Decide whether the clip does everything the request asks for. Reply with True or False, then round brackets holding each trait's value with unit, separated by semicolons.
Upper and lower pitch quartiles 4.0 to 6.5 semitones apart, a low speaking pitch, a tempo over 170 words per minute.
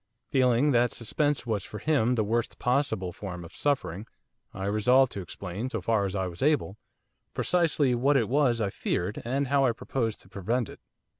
True (5.1 semitones; 120 Hz; 190 wpm)